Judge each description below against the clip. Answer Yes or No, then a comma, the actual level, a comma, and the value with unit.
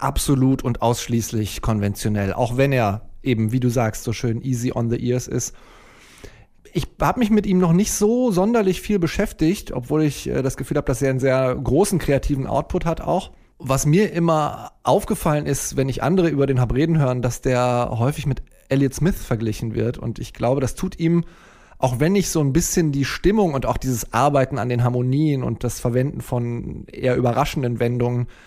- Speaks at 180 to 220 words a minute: Yes, fast, 190 wpm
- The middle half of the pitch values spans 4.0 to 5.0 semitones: Yes, average, 4.5 semitones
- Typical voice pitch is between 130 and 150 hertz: Yes, low, 135 Hz